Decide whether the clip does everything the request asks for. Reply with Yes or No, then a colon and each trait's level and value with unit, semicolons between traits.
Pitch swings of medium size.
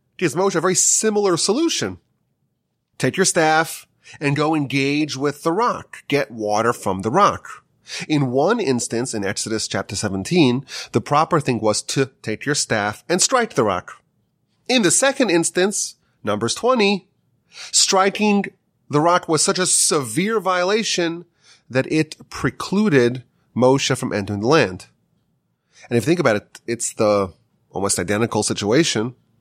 No: wide, 7.5 semitones